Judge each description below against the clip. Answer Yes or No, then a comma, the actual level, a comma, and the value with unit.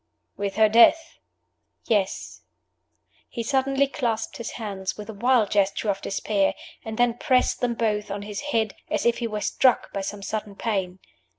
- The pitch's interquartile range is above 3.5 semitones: No, average, 2.9 semitones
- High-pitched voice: Yes, high, 220 Hz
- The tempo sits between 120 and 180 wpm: Yes, average, 170 wpm